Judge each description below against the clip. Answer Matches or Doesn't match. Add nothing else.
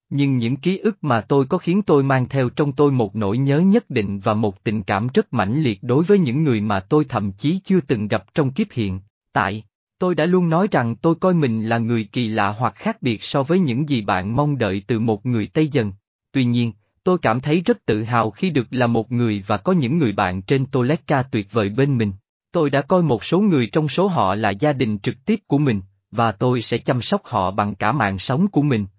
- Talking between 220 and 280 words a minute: Matches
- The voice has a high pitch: Doesn't match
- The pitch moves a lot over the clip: Matches